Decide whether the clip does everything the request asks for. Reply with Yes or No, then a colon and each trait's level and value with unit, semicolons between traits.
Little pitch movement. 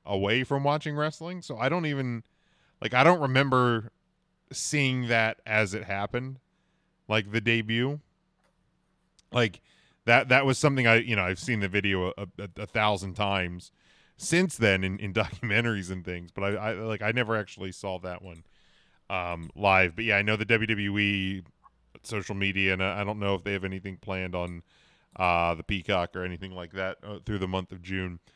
No: average, 3.8 semitones